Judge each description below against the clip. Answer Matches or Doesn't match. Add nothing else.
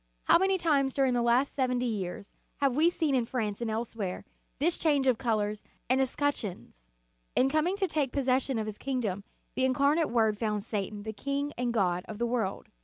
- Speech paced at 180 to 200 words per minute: Matches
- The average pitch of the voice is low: Doesn't match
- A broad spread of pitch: Doesn't match